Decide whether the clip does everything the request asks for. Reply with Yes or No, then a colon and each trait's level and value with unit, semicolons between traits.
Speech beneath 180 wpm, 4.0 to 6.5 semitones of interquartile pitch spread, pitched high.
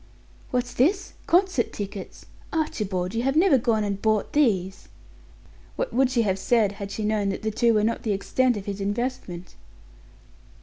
Yes: average, 170 wpm; average, 4.3 semitones; high, 220 Hz